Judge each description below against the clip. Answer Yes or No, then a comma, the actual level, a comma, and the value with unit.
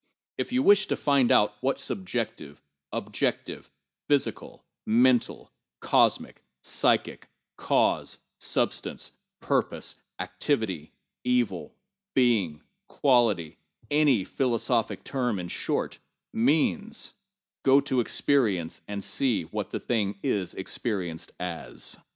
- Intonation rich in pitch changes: Yes, wide, 5.9 semitones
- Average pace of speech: No, slow, 100 wpm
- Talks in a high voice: No, low, 120 Hz